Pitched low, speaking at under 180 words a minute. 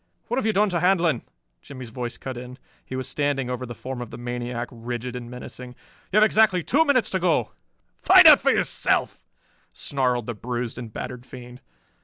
No: low, 125 Hz; average, 195 wpm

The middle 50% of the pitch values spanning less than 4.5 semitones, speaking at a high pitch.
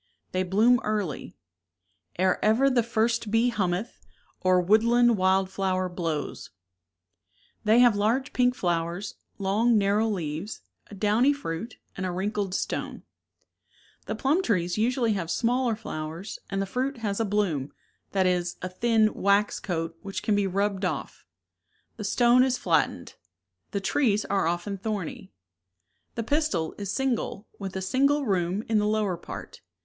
Yes: average, 3.9 semitones; high, 205 Hz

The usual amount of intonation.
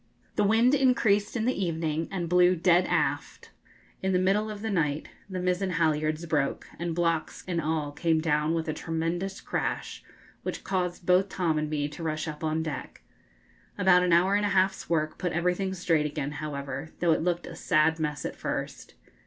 Yes: average, 3.1 semitones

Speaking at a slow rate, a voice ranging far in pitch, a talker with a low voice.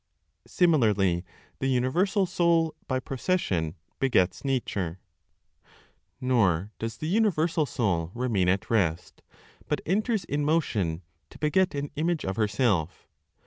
Yes: slow, 115 wpm; wide, 9.0 semitones; low, 130 Hz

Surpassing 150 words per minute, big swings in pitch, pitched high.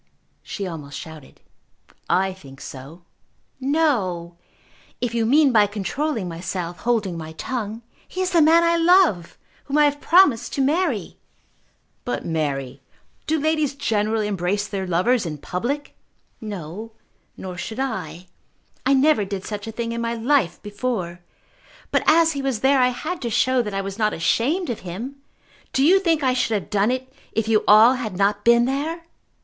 Yes: average, 170 wpm; wide, 6.7 semitones; high, 225 Hz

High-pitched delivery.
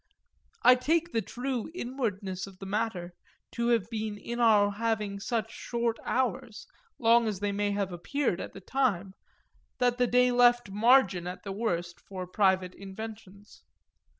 Yes: high, 215 Hz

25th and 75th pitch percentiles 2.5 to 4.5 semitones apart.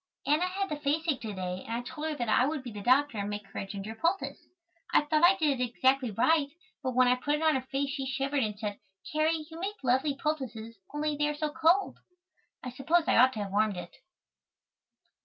No: average, 5.0 semitones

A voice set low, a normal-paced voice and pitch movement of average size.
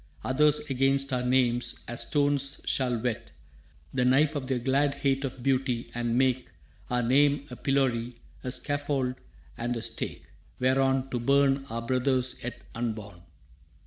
No: low, 130 Hz; average, 145 wpm; narrow, 2.1 semitones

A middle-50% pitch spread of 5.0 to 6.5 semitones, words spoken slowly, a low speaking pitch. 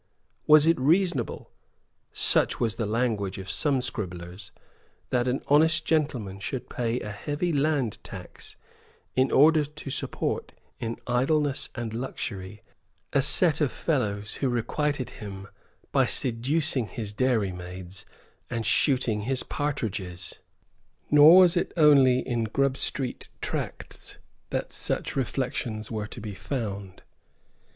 Yes: wide, 5.5 semitones; slow, 130 wpm; low, 125 Hz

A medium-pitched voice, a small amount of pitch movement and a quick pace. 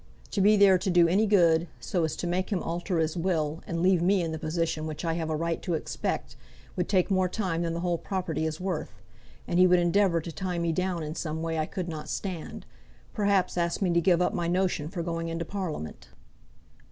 Yes: medium, 170 Hz; narrow, 2.2 semitones; fast, 230 wpm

